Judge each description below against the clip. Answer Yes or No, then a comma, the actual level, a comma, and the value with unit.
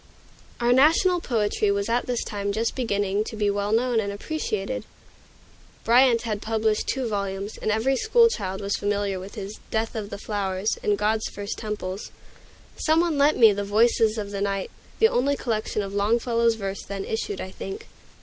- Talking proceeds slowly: No, average, 180 wpm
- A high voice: Yes, high, 215 Hz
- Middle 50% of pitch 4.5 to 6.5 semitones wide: No, average, 2.9 semitones